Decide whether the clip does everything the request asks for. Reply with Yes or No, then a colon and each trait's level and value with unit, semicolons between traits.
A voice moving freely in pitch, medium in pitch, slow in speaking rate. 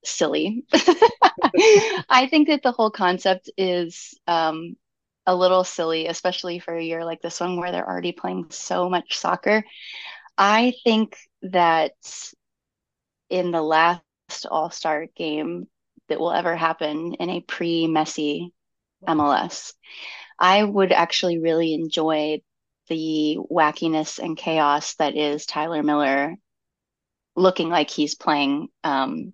No: average, 3.1 semitones; medium, 170 Hz; slow, 125 wpm